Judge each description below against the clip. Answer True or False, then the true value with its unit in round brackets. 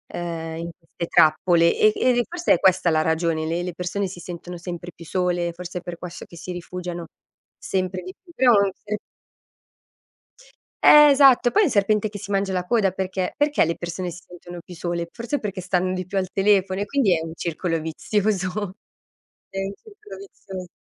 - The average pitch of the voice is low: False (185 Hz)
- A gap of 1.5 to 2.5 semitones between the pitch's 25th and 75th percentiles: False (2.9 semitones)